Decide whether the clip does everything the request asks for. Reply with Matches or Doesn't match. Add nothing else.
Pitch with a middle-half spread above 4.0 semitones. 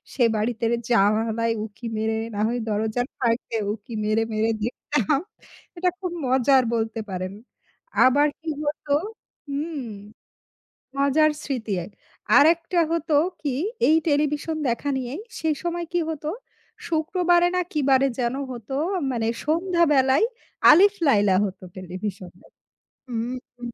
Matches